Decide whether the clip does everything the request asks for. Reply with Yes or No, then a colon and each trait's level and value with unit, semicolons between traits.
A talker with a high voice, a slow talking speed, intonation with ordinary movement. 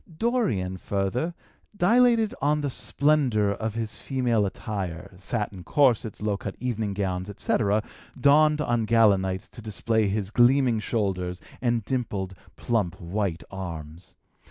No: low, 110 Hz; slow, 130 wpm; average, 4.7 semitones